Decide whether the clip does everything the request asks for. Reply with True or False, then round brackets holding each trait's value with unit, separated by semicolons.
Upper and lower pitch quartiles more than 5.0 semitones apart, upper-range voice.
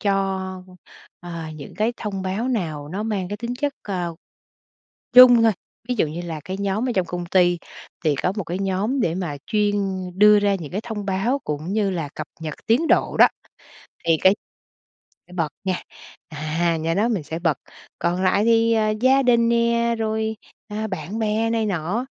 False (4.4 semitones; 195 Hz)